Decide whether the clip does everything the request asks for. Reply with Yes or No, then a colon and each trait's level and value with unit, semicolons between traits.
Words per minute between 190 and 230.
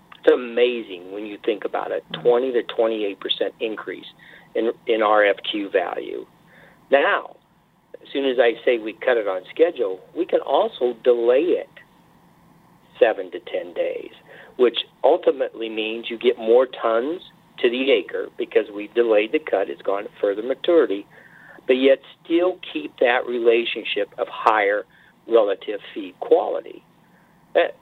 No: average, 145 wpm